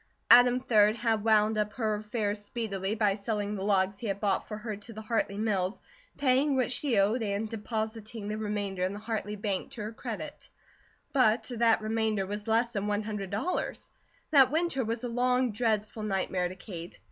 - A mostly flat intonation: Yes, narrow, 2.2 semitones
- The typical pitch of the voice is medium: No, high, 215 Hz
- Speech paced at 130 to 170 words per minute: No, average, 190 wpm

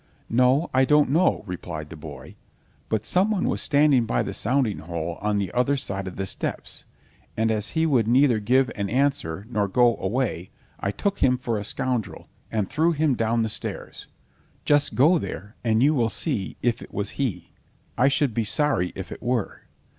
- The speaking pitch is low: Yes, low, 120 Hz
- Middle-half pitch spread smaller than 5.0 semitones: No, wide, 5.4 semitones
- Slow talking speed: No, average, 185 wpm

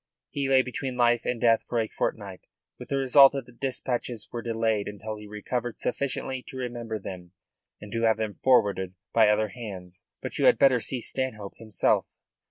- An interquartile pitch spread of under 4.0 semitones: Yes, average, 3.2 semitones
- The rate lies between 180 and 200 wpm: Yes, average, 185 wpm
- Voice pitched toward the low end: Yes, low, 115 Hz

